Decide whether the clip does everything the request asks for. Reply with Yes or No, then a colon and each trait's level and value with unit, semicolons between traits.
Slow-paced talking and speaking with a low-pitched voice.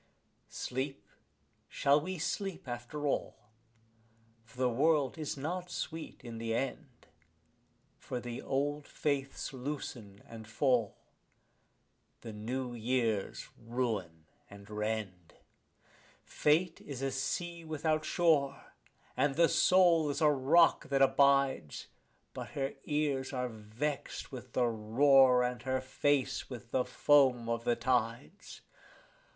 Yes: slow, 120 wpm; low, 130 Hz